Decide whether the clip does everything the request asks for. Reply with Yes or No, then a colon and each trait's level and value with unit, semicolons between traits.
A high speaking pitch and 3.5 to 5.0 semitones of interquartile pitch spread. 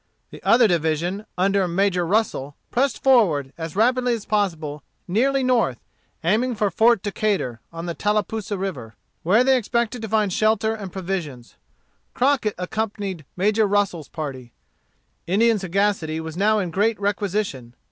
Yes: high, 200 Hz; average, 4.6 semitones